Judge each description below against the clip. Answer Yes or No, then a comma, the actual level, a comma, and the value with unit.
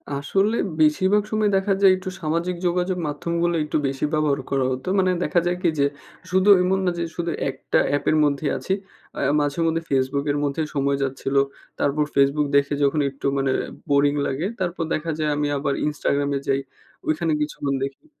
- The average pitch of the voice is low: No, medium, 150 Hz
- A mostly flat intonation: No, average, 3.9 semitones